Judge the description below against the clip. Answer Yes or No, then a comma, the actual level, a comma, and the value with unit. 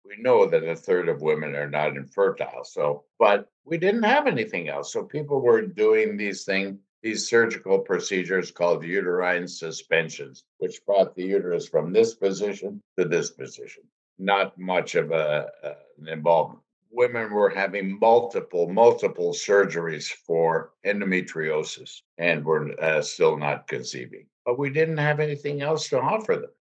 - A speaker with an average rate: Yes, average, 155 wpm